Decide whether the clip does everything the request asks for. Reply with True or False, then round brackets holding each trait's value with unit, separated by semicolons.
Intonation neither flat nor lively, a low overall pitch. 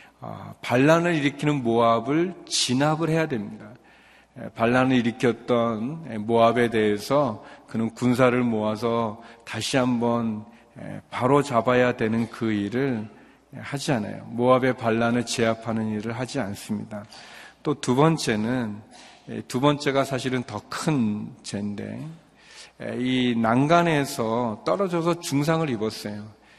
True (3.6 semitones; 120 Hz)